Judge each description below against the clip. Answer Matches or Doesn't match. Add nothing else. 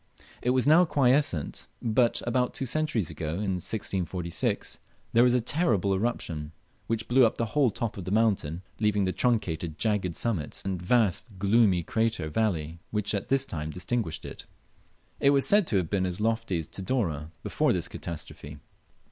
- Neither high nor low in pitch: Doesn't match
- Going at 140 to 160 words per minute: Doesn't match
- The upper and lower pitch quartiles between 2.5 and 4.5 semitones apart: Doesn't match